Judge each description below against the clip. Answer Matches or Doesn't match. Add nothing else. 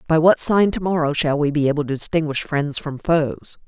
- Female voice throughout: Matches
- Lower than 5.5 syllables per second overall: Matches